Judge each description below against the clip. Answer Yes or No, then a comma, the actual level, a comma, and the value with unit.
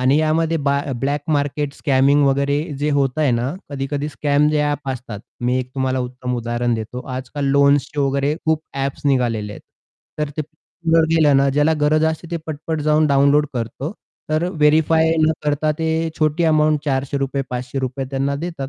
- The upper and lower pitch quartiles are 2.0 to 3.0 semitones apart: Yes, narrow, 2.4 semitones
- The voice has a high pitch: No, medium, 140 Hz